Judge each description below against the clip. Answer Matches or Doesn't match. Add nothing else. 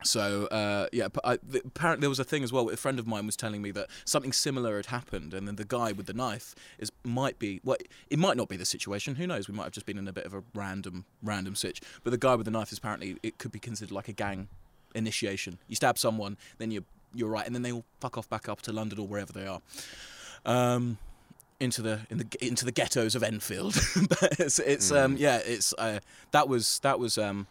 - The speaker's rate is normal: Doesn't match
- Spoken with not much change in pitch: Doesn't match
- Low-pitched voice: Matches